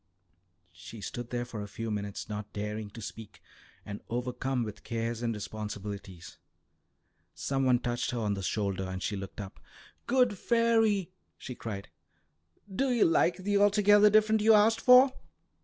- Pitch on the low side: Yes, low, 120 Hz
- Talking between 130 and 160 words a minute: Yes, average, 155 wpm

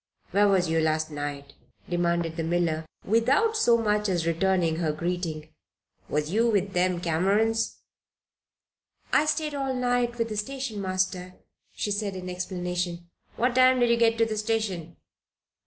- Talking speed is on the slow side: No, average, 155 wpm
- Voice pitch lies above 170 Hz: Yes, high, 190 Hz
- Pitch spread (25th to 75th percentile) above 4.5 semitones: Yes, average, 5.0 semitones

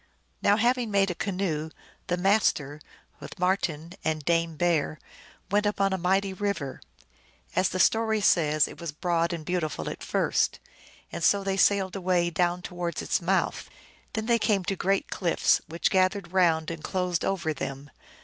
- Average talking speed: Yes, average, 165 wpm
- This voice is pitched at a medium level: Yes, medium, 180 Hz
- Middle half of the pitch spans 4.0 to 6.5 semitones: No, average, 2.9 semitones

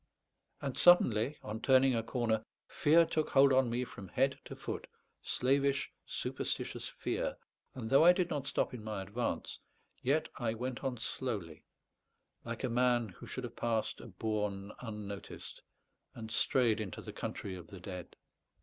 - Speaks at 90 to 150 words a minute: No, average, 160 wpm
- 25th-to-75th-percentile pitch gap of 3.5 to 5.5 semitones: Yes, average, 3.9 semitones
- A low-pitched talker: Yes, low, 120 Hz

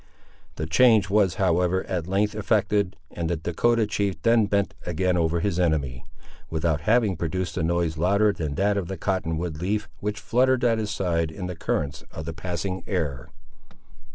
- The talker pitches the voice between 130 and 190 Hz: No, very low, 90 Hz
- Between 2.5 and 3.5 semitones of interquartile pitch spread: No, average, 4.0 semitones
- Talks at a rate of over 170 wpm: Yes, average, 180 wpm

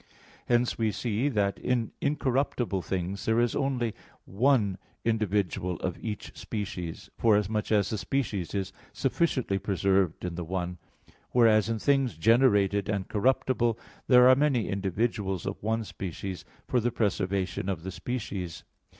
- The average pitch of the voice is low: Yes, low, 105 Hz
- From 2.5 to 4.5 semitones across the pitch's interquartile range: Yes, average, 3.9 semitones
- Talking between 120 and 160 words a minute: Yes, average, 140 wpm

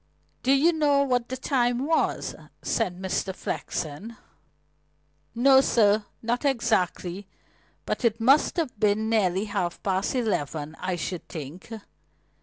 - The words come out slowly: Yes, slow, 125 wpm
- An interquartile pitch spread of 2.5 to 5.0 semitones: No, wide, 5.6 semitones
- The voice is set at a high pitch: Yes, high, 220 Hz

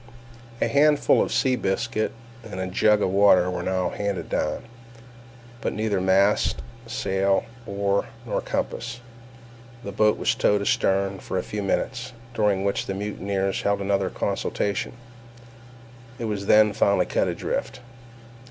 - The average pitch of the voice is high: No, low, 100 Hz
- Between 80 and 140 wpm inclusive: Yes, slow, 135 wpm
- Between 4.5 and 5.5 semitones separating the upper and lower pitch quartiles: No, average, 3.2 semitones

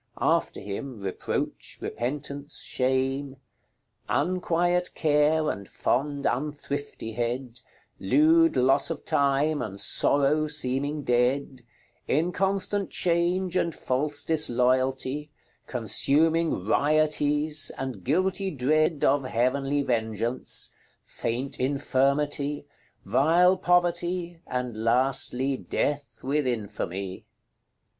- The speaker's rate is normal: No, slow, 85 wpm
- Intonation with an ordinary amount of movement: Yes, average, 3.5 semitones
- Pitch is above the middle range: No, medium, 140 Hz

